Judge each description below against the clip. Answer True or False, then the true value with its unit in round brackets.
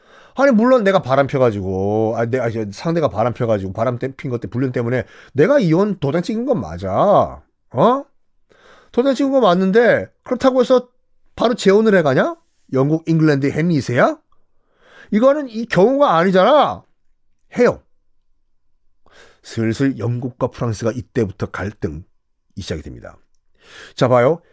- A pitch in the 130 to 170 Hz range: True (135 Hz)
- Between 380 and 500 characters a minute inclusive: False (285 characters per minute)